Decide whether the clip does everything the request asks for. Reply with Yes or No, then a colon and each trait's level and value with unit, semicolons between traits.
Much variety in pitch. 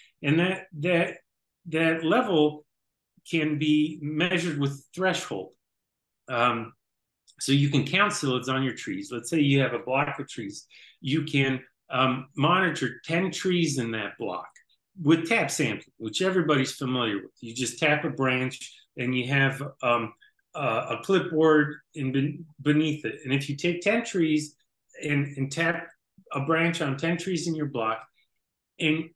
No: average, 3.8 semitones